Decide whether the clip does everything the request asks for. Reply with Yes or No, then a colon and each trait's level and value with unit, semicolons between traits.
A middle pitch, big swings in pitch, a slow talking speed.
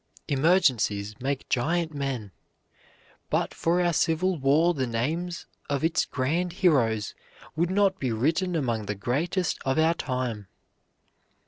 Yes: medium, 145 Hz; wide, 5.8 semitones; slow, 130 wpm